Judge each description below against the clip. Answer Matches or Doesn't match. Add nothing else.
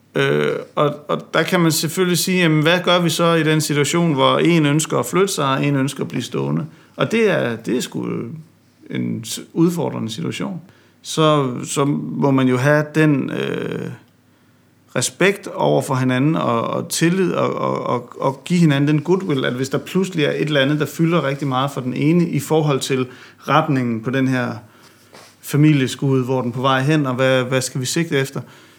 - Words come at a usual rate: Matches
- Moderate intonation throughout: Matches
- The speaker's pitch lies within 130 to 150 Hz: Matches